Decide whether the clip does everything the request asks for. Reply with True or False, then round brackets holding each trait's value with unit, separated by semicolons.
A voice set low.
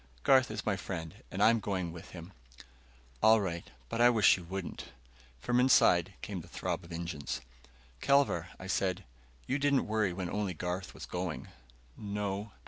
True (95 Hz)